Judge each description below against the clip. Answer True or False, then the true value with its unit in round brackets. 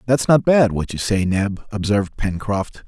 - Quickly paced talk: False (190 wpm)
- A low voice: True (105 Hz)